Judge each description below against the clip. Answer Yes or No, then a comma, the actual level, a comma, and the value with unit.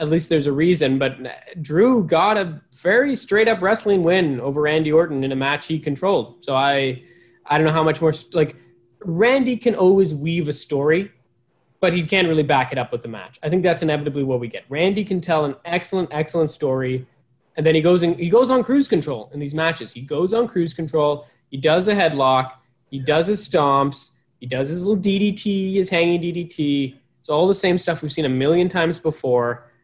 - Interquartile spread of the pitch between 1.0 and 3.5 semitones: No, average, 4.6 semitones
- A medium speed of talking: No, fast, 210 wpm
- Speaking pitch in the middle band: Yes, medium, 160 Hz